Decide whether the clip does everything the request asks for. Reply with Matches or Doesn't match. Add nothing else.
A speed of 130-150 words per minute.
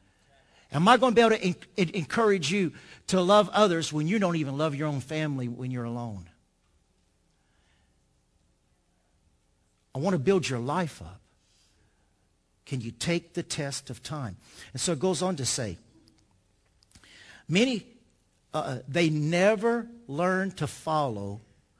Matches